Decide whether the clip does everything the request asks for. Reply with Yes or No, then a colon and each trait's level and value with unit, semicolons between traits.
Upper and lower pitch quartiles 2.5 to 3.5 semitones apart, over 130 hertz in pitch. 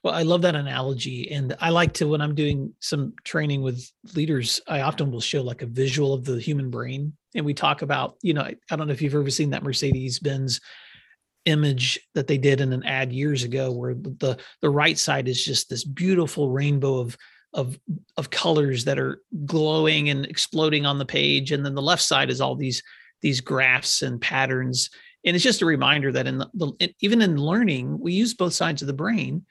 Yes: average, 3.1 semitones; medium, 140 Hz